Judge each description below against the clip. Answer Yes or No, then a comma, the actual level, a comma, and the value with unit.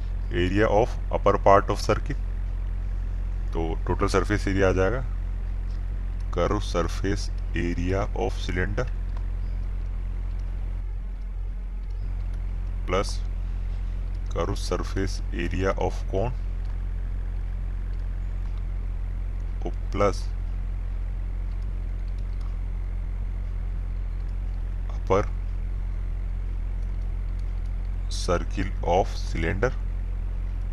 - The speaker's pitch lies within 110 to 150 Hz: No, very low, 90 Hz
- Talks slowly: Yes, slow, 55 wpm